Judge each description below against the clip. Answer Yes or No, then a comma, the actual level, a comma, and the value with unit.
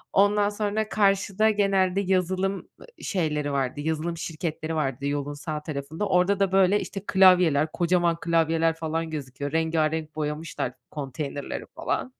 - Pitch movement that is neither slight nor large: Yes, average, 4.1 semitones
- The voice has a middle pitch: Yes, medium, 165 Hz